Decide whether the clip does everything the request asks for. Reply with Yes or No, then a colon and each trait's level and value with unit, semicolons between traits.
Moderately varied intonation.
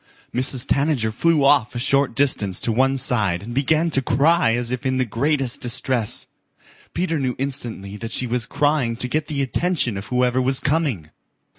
Yes: average, 3.3 semitones